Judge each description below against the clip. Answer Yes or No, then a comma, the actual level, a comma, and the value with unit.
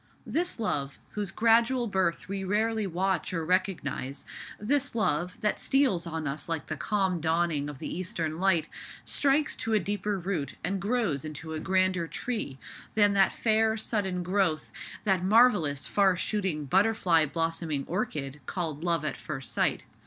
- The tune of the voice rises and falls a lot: No, average, 4.8 semitones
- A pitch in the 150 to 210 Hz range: Yes, medium, 185 Hz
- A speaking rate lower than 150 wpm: No, average, 155 wpm